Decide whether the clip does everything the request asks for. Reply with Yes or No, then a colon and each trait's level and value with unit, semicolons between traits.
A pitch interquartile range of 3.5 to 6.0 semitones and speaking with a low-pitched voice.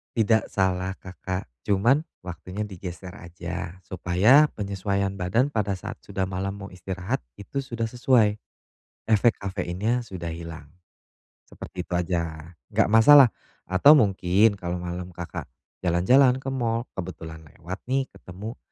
Yes: average, 4.0 semitones; very low, 95 Hz